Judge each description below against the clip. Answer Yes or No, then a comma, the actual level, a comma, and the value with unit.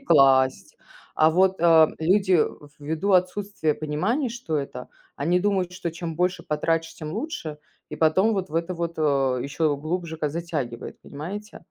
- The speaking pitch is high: No, medium, 165 Hz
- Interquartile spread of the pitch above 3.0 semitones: Yes, average, 3.5 semitones